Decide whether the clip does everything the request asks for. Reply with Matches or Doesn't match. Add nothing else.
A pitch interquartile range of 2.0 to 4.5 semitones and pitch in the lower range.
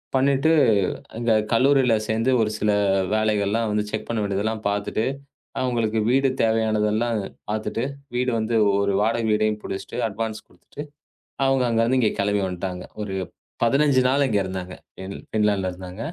Matches